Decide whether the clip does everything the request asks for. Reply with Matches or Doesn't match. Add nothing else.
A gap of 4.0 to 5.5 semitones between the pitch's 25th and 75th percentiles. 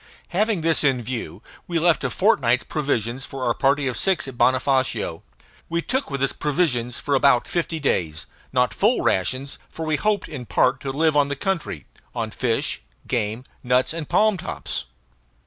Matches